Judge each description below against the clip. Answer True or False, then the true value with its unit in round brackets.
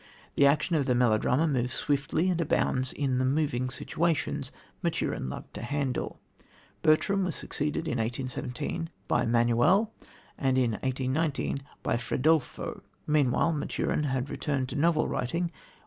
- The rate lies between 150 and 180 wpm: False (135 wpm)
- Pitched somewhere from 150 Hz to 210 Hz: False (140 Hz)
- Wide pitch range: False (3.9 semitones)